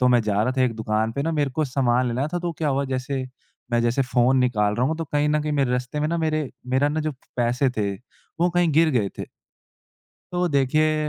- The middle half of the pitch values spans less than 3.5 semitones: No, average, 3.8 semitones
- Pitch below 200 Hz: Yes, low, 135 Hz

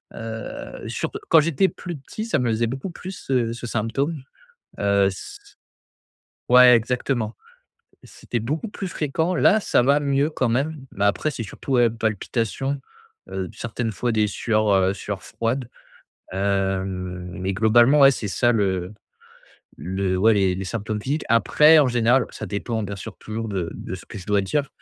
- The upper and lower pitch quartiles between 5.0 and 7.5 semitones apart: Yes, average, 5.3 semitones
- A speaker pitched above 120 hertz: No, low, 115 Hz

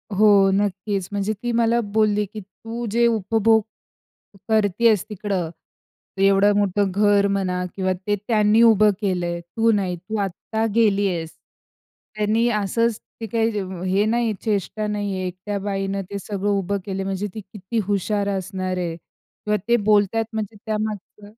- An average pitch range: No, narrow, 2.0 semitones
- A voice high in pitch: Yes, high, 205 Hz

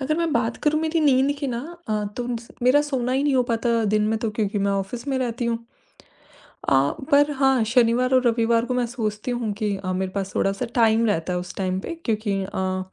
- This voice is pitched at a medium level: No, high, 235 Hz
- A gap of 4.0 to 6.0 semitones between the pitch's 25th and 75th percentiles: No, average, 3.5 semitones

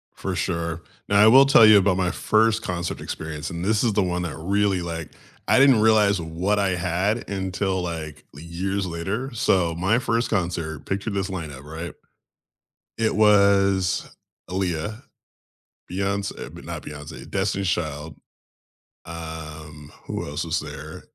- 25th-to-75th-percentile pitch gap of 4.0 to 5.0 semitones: No, average, 3.6 semitones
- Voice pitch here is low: Yes, very low, 95 Hz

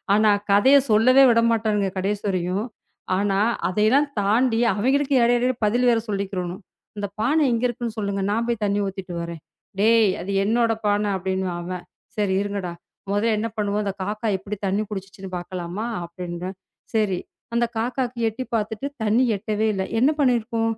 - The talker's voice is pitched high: Yes, high, 210 Hz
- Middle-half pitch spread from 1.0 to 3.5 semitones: Yes, average, 3.0 semitones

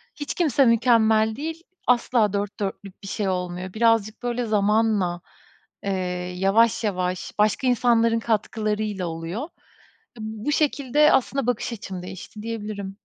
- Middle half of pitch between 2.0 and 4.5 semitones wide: Yes, average, 3.2 semitones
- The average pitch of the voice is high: Yes, high, 220 Hz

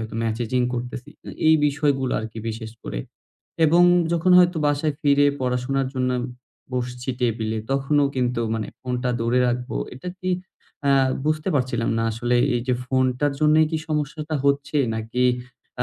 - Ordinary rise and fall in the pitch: Yes, average, 3.1 semitones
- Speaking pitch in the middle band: No, low, 130 Hz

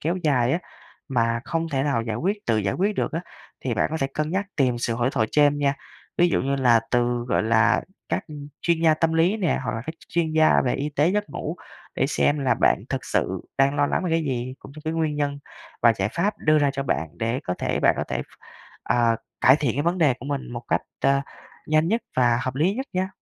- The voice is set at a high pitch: No, medium, 145 Hz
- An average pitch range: Yes, average, 5.0 semitones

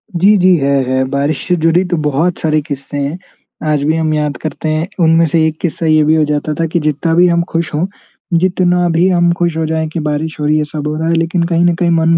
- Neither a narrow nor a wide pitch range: No, narrow, 2.2 semitones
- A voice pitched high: No, medium, 160 Hz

